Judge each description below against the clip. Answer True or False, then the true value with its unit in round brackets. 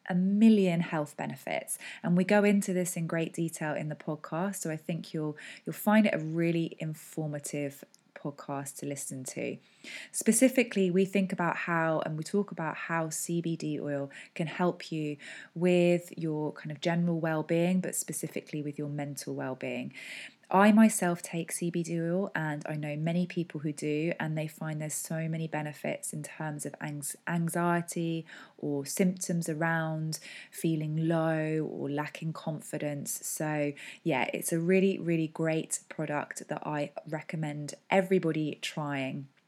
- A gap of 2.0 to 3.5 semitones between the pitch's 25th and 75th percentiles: True (2.6 semitones)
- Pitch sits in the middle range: True (160 Hz)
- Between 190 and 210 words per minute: False (150 wpm)